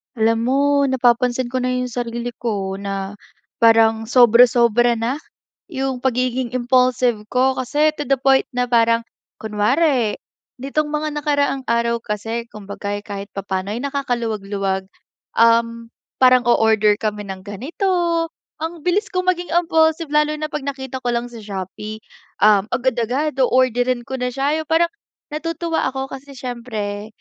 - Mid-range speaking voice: No, high, 245 Hz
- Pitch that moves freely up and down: No, average, 3.6 semitones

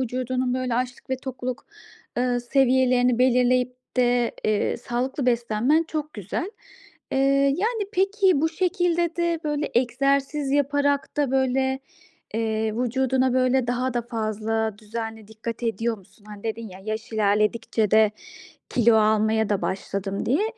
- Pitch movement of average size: Yes, average, 3.3 semitones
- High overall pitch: Yes, high, 245 Hz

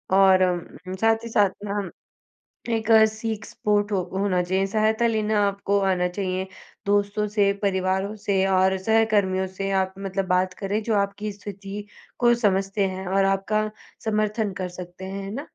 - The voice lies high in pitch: Yes, high, 200 Hz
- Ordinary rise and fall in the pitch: No, narrow, 2.0 semitones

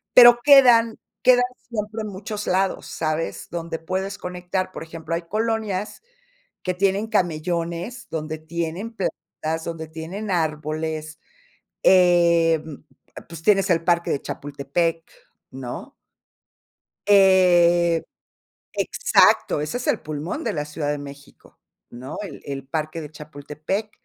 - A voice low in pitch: No, medium, 170 Hz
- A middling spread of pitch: Yes, average, 3.9 semitones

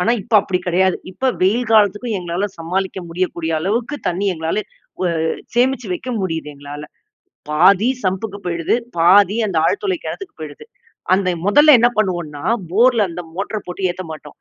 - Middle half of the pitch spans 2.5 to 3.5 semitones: No, average, 4.2 semitones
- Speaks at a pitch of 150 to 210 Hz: Yes, high, 190 Hz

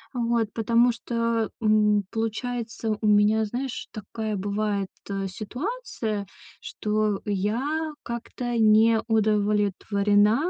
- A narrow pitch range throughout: Yes, narrow, 2.0 semitones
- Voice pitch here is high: Yes, high, 220 Hz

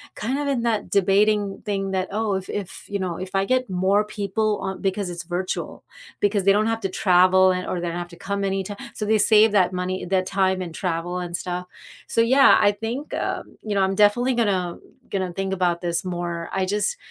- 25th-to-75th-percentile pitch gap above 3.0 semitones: No, narrow, 2.4 semitones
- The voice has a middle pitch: No, high, 195 Hz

